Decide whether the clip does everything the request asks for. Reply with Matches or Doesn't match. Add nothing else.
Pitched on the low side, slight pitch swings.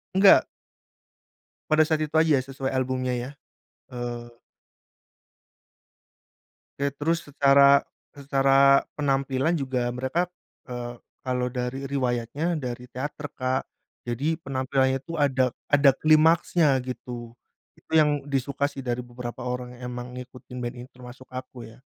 Matches